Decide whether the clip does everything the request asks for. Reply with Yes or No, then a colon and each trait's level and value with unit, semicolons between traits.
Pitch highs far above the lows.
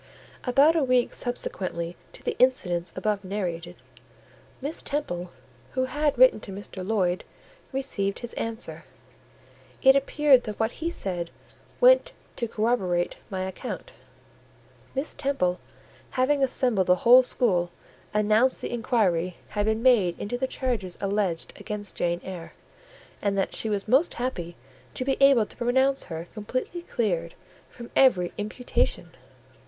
Yes: wide, 5.9 semitones